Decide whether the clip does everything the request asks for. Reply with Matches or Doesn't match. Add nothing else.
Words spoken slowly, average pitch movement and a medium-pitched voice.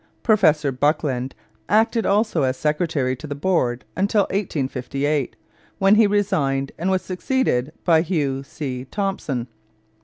Doesn't match